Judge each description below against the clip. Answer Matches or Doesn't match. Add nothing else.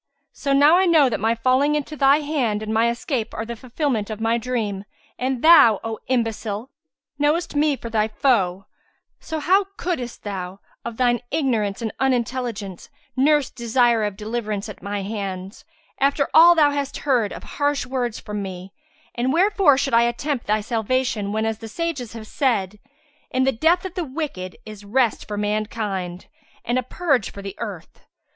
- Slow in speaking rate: Doesn't match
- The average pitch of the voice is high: Matches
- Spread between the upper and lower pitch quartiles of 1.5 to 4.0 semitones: Doesn't match